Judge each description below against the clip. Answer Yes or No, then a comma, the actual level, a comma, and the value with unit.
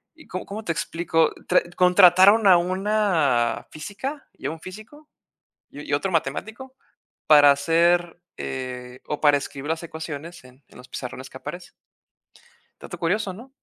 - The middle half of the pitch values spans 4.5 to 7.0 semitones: Yes, average, 5.3 semitones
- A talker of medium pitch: Yes, medium, 170 Hz